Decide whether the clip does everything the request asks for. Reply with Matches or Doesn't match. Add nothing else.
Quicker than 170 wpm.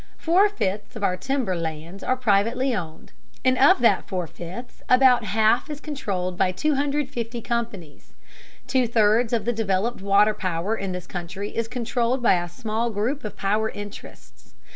Doesn't match